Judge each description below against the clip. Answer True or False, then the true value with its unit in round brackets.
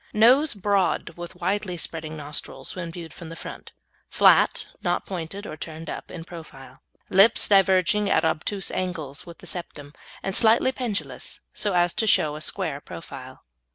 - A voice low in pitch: False (175 Hz)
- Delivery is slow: False (160 wpm)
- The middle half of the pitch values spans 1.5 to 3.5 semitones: False (4.0 semitones)